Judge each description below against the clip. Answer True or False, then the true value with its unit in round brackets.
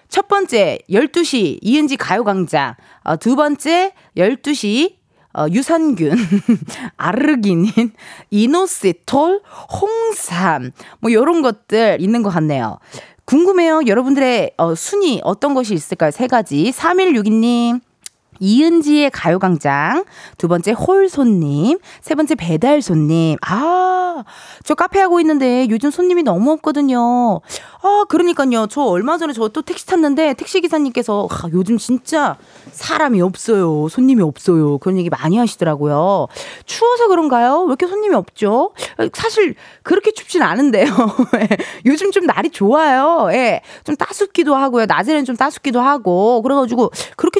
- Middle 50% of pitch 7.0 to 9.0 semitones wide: True (8.5 semitones)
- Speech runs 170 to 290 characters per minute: True (280 characters per minute)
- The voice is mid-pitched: False (255 Hz)